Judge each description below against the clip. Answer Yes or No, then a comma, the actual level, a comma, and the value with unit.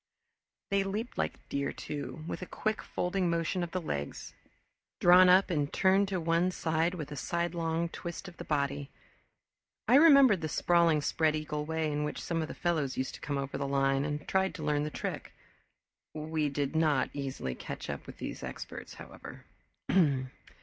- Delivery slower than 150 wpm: No, average, 180 wpm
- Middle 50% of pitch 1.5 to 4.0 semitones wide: Yes, average, 3.3 semitones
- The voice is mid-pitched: Yes, medium, 160 Hz